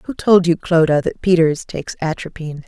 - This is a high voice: No, medium, 170 Hz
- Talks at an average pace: Yes, average, 180 wpm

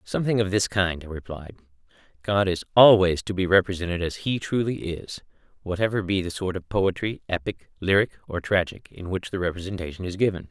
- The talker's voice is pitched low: Yes, very low, 95 Hz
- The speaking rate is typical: Yes, average, 175 wpm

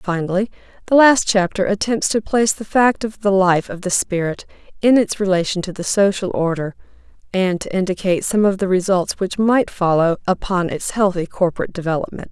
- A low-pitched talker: No, high, 195 Hz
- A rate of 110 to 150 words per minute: No, average, 180 wpm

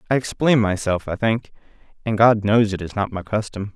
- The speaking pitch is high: No, low, 105 Hz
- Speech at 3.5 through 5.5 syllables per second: Yes, 5.3 syllables/s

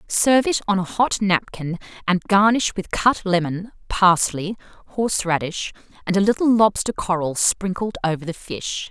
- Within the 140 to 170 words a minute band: Yes, average, 150 wpm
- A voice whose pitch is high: Yes, high, 195 Hz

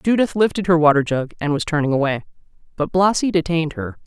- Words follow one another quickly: No, average, 190 wpm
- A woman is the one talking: Yes, female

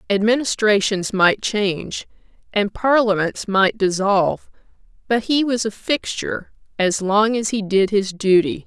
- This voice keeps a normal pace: No, slow, 130 wpm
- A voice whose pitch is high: Yes, high, 205 Hz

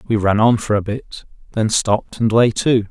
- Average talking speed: No, fast, 225 wpm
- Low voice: Yes, low, 110 Hz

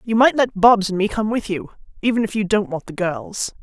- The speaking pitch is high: Yes, high, 205 Hz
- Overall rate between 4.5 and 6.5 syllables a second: Yes, 5.3 syllables/s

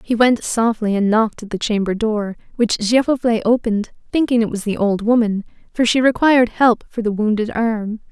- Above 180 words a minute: Yes, average, 190 wpm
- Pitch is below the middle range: No, high, 225 Hz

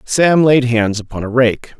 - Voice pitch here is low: Yes, low, 125 Hz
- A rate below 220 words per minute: Yes, average, 200 wpm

